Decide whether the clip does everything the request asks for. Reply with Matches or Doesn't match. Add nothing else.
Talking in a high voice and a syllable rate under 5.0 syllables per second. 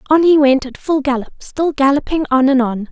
Doesn't match